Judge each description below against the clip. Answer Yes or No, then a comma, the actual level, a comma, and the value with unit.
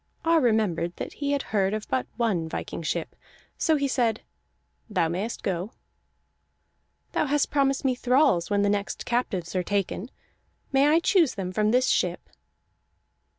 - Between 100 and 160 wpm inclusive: Yes, average, 155 wpm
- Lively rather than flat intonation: Yes, wide, 6.2 semitones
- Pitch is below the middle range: No, high, 220 Hz